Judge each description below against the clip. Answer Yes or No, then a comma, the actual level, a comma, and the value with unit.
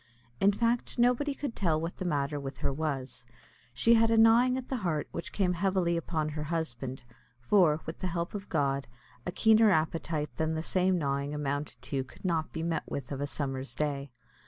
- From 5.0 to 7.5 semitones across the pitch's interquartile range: Yes, average, 5.3 semitones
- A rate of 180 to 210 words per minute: Yes, average, 200 wpm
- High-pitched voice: No, medium, 160 Hz